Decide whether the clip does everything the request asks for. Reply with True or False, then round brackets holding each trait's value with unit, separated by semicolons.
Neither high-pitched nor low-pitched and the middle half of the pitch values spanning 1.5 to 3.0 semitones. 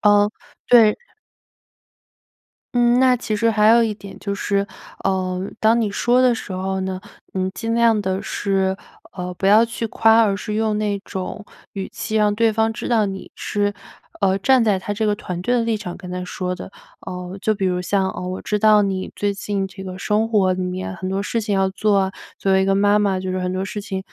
False (200 Hz; 2.4 semitones)